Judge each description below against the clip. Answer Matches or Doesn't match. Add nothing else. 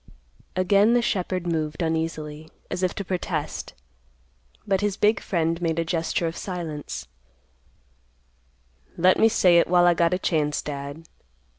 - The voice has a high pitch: Doesn't match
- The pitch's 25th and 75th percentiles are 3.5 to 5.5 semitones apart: Doesn't match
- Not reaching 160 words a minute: Matches